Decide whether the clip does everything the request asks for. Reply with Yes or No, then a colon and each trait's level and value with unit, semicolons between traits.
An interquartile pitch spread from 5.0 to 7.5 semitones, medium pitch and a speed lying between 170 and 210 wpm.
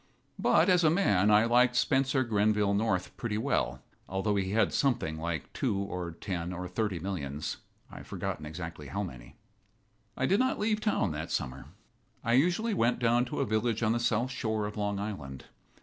No: average, 5.3 semitones; low, 105 Hz; average, 180 wpm